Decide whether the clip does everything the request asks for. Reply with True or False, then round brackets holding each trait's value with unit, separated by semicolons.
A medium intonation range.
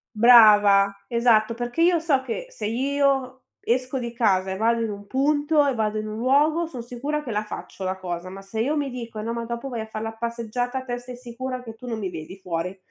True (3.4 semitones)